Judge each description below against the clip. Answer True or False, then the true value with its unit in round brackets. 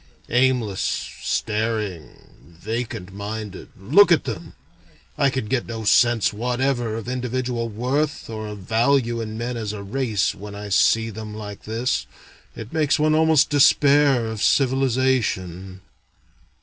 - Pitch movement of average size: True (3.8 semitones)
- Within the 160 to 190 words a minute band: False (135 wpm)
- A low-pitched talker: True (115 Hz)